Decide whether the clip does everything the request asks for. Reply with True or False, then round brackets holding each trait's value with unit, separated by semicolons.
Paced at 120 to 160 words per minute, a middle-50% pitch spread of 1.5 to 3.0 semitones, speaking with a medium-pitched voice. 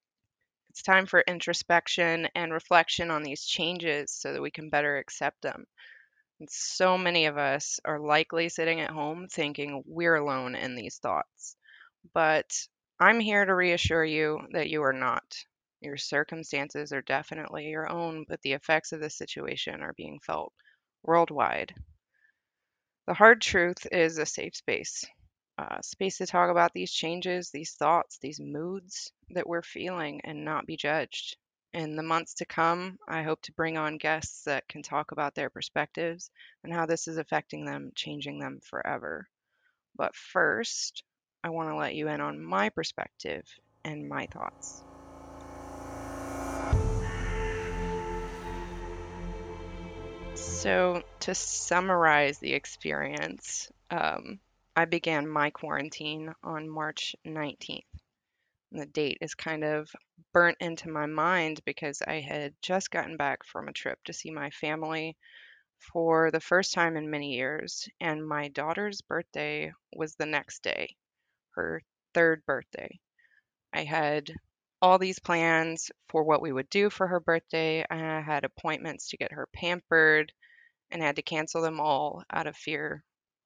True (145 wpm; 2.7 semitones; 160 Hz)